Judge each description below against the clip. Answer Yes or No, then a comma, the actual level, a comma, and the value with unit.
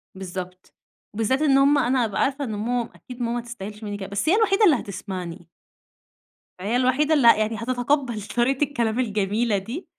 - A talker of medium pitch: No, high, 235 Hz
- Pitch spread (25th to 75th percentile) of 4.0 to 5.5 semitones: Yes, average, 4.6 semitones